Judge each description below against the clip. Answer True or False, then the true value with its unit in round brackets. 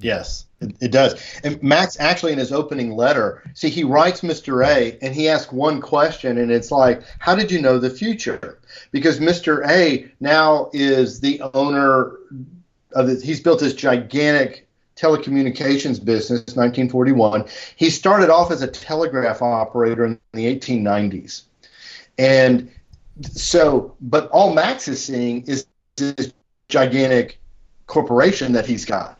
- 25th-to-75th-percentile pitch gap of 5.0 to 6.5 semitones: False (3.7 semitones)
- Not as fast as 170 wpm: True (150 wpm)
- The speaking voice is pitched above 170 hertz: False (135 Hz)